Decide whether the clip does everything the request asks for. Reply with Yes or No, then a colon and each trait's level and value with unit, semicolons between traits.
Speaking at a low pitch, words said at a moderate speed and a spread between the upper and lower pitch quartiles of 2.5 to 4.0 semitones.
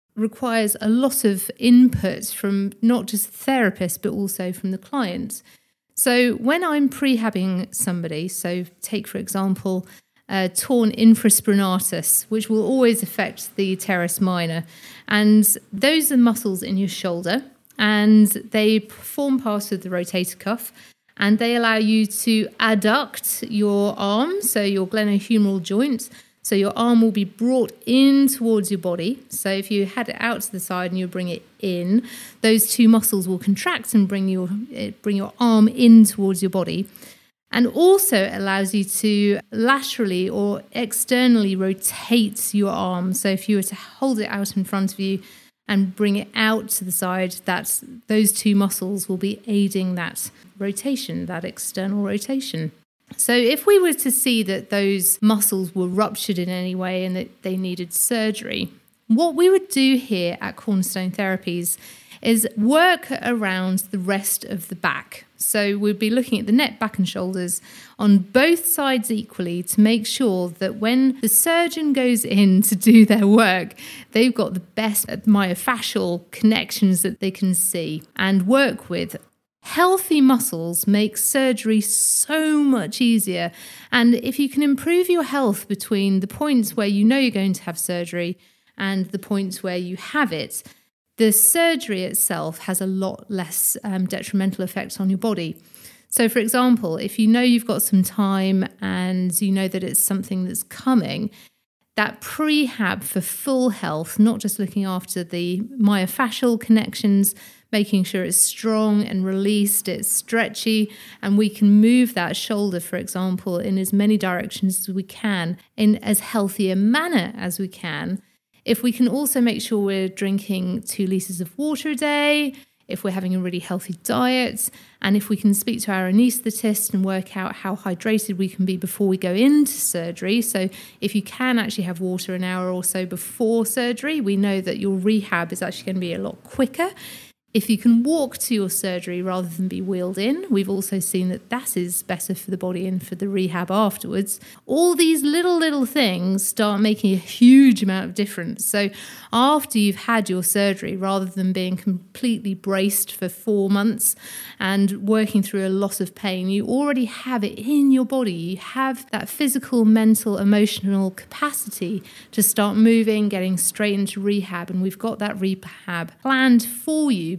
No: high, 205 Hz; average, 170 wpm; average, 3.5 semitones